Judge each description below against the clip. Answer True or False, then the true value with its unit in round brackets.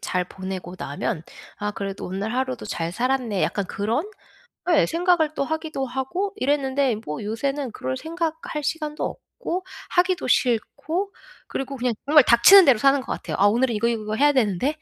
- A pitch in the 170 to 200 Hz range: False (260 Hz)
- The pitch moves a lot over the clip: True (6.3 semitones)